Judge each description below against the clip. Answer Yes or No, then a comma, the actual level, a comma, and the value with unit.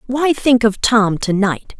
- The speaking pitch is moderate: No, high, 230 Hz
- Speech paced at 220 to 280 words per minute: No, average, 200 wpm